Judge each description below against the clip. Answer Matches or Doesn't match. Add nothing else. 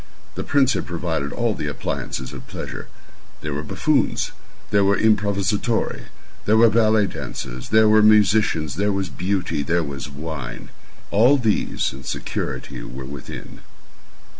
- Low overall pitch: Matches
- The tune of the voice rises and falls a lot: Matches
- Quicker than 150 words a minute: Doesn't match